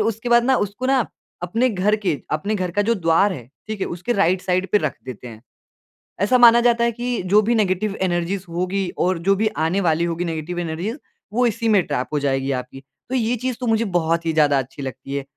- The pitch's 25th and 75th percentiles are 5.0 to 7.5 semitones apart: Yes, wide, 5.4 semitones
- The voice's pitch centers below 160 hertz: No, high, 190 Hz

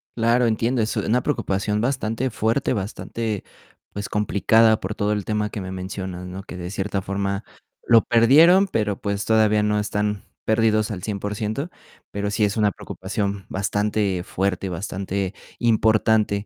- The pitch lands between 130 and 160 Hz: No, low, 105 Hz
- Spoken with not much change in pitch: Yes, narrow, 2.1 semitones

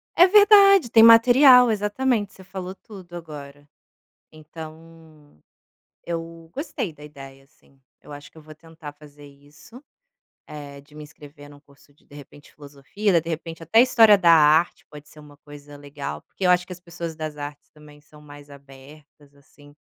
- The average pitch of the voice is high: No, medium, 155 Hz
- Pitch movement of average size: Yes, average, 3.9 semitones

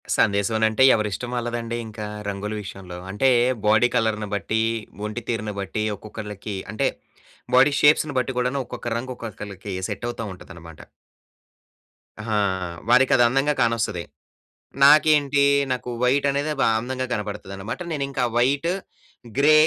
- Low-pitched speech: Yes, low, 115 Hz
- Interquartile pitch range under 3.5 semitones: No, average, 4.0 semitones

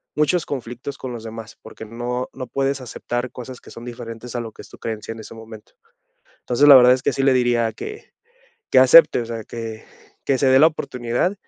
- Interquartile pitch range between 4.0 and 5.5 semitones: No, narrow, 2.6 semitones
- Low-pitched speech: Yes, low, 120 Hz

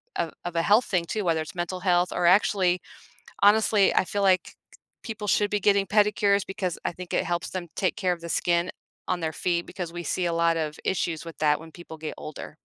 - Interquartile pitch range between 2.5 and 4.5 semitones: Yes, average, 2.9 semitones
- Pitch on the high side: No, medium, 180 Hz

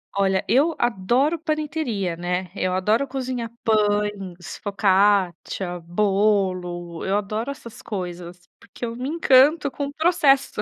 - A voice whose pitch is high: Yes, high, 210 Hz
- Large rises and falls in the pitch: Yes, wide, 6.0 semitones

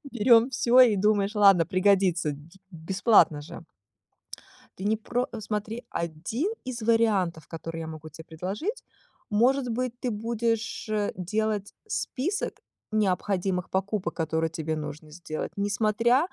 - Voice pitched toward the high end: Yes, high, 205 Hz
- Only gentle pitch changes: No, average, 5.3 semitones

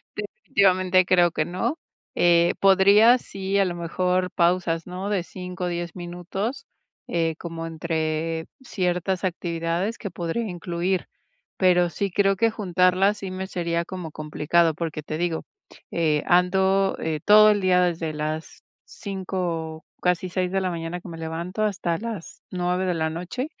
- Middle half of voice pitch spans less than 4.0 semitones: Yes, narrow, 2.4 semitones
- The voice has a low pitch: No, medium, 180 Hz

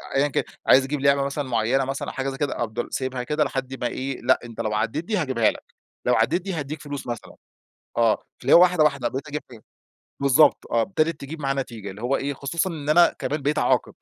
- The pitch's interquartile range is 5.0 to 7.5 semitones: No, average, 3.3 semitones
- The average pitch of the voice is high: No, low, 135 Hz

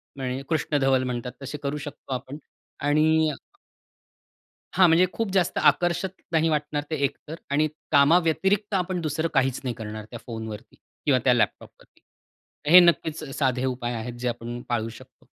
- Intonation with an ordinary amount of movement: Yes, average, 4.4 semitones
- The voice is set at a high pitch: No, medium, 140 Hz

